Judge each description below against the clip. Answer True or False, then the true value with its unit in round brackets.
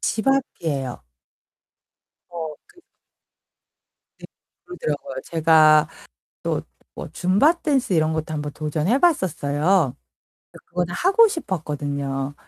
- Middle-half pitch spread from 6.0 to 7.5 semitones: True (6.6 semitones)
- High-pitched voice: False (160 Hz)